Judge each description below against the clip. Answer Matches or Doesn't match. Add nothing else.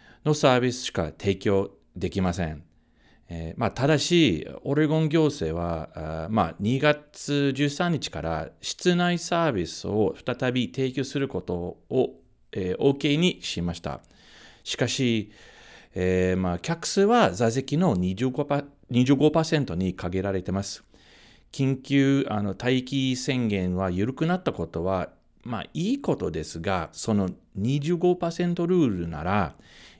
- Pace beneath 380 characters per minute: Matches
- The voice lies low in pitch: Matches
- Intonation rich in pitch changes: Matches